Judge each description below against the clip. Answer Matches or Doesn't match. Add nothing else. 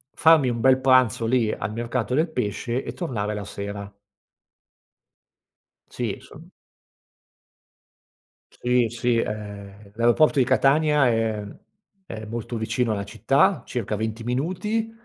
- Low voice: Matches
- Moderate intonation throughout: Matches